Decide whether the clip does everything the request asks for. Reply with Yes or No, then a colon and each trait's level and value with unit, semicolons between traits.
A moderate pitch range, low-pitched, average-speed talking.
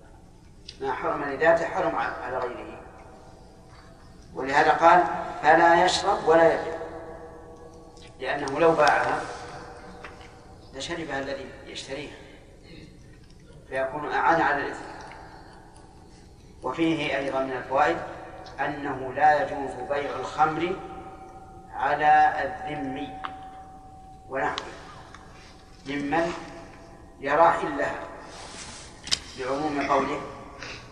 No: average, 3.2 semitones; medium, 150 Hz; average, 75 wpm